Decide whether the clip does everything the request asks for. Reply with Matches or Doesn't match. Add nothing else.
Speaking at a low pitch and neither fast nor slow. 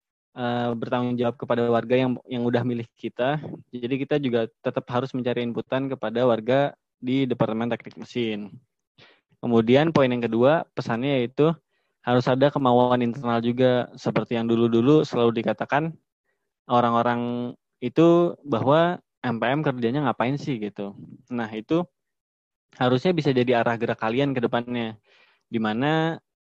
Matches